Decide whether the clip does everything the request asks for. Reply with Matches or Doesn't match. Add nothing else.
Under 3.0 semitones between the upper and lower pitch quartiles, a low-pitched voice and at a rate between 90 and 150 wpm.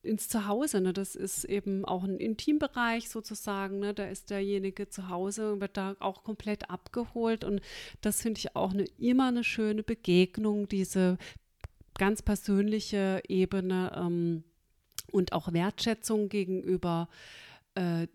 Doesn't match